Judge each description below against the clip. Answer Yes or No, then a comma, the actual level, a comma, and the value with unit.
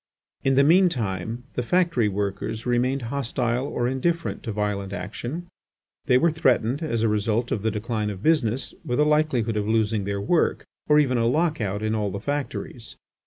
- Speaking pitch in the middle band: No, low, 120 Hz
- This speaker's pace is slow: No, average, 185 wpm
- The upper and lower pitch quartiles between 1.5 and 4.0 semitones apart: No, average, 4.9 semitones